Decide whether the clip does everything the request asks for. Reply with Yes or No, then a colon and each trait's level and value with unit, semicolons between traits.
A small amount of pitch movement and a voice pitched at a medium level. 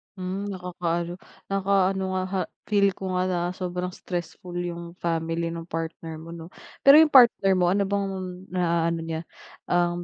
Yes: narrow, 2.2 semitones; medium, 180 Hz